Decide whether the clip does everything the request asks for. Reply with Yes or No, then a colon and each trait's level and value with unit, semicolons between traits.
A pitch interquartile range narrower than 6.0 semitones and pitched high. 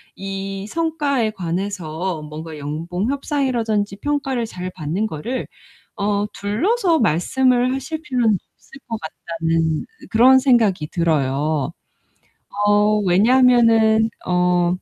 No: wide, 6.9 semitones; high, 205 Hz